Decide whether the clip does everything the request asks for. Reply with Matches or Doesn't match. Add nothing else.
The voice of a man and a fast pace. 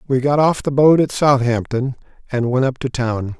Matches